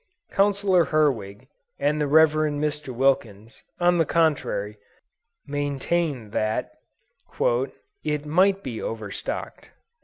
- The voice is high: No, medium, 145 Hz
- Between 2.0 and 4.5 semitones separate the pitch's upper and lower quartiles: No, average, 5.3 semitones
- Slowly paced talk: Yes, slow, 95 wpm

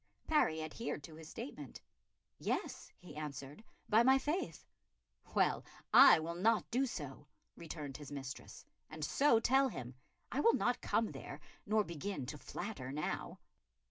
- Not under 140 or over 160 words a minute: Yes, average, 145 wpm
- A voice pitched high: No, medium, 160 Hz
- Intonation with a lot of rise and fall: Yes, wide, 7.8 semitones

